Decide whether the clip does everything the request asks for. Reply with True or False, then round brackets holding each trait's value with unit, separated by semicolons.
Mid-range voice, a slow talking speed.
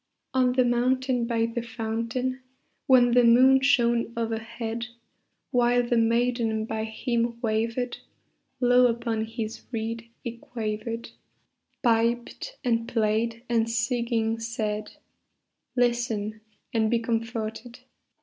False (235 Hz; 110 wpm)